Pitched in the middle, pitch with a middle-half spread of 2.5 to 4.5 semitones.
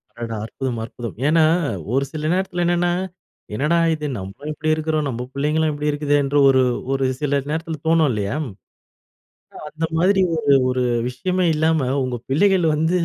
Yes: medium, 150 Hz; average, 3.4 semitones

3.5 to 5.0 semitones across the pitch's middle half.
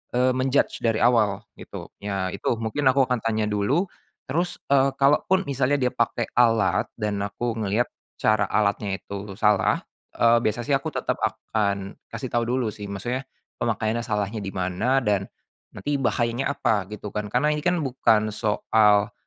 Yes: average, 3.9 semitones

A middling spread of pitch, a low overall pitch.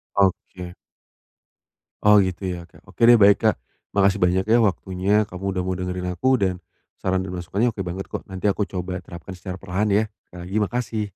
No: narrow, 2.3 semitones; very low, 95 Hz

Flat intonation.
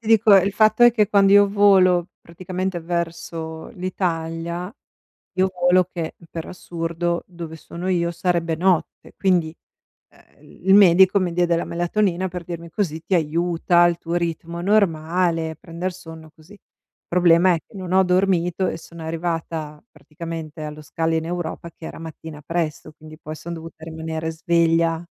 Yes: narrow, 2.1 semitones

